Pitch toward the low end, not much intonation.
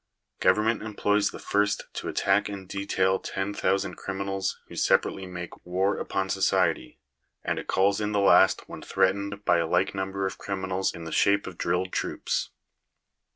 Yes: very low, 95 Hz; narrow, 1.3 semitones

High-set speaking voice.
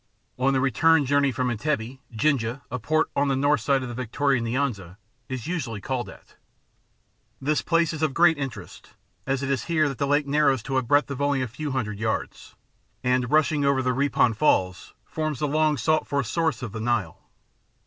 No: low, 135 Hz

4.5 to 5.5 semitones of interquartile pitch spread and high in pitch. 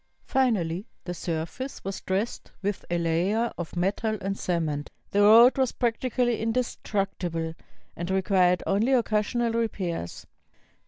Yes: average, 4.8 semitones; high, 195 Hz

